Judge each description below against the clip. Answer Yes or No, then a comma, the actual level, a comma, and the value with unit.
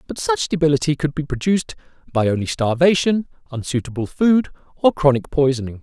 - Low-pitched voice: No, medium, 150 Hz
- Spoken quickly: No, average, 145 wpm